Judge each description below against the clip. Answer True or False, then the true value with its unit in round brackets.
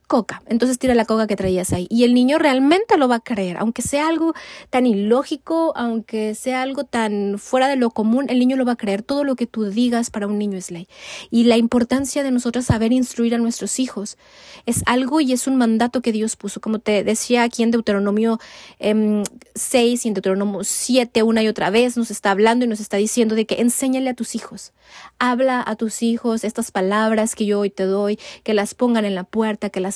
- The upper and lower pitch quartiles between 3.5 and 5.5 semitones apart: False (3.0 semitones)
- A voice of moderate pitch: False (230 Hz)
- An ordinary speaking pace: False (220 wpm)